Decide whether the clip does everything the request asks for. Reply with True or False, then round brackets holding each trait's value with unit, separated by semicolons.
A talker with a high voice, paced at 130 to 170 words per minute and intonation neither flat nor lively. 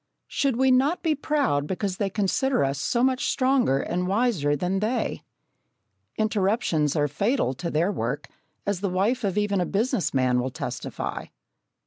False (200 Hz; 160 wpm; 8.4 semitones)